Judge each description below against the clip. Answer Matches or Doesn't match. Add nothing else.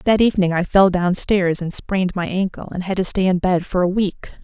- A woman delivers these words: Matches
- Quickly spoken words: Matches